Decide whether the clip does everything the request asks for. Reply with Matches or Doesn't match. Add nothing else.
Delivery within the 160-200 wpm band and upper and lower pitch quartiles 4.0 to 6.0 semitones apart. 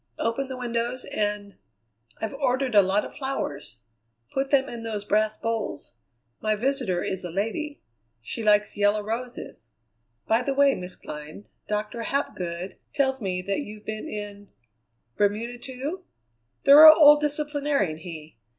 Doesn't match